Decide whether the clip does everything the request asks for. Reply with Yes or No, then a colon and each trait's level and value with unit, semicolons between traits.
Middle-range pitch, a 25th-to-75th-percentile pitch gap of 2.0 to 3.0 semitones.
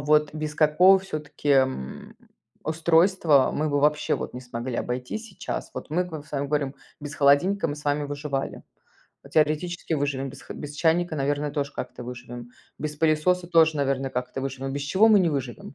Yes: medium, 150 Hz; average, 2.7 semitones